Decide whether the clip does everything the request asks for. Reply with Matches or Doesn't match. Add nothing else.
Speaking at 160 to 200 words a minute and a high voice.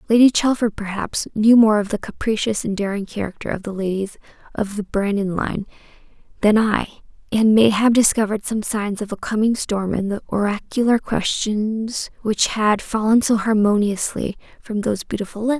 Matches